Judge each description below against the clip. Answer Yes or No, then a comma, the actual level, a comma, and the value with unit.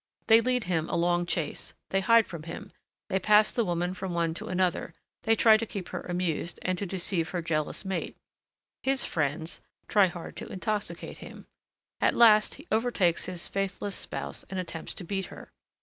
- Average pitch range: Yes, average, 3.7 semitones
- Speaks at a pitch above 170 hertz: Yes, medium, 185 Hz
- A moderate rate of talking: Yes, average, 185 wpm